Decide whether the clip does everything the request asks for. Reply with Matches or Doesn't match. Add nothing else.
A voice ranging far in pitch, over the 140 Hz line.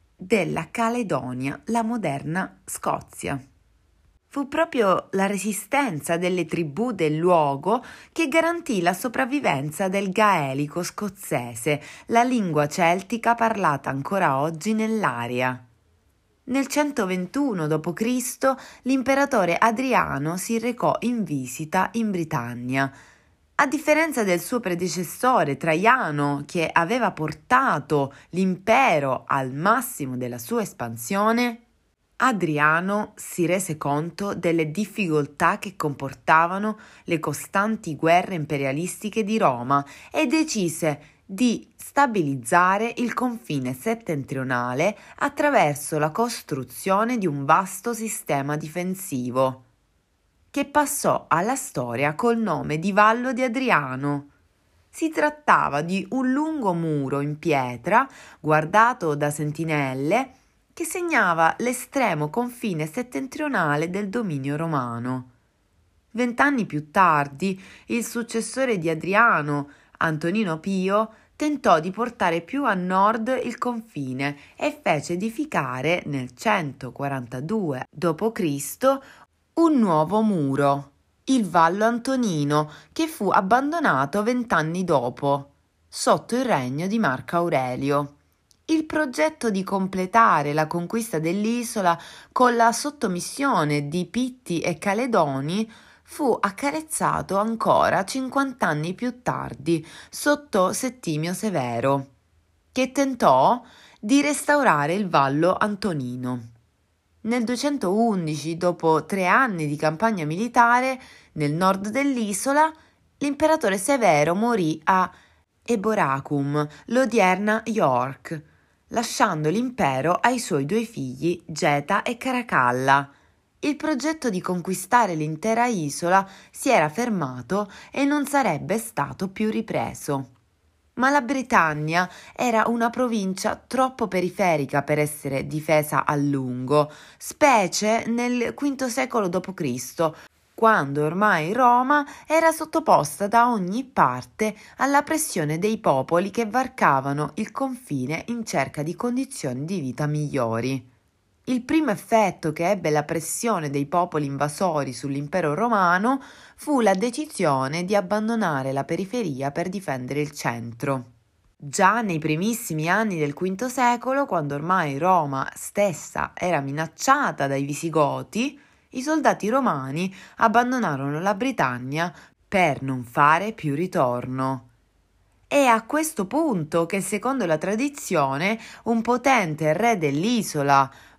Matches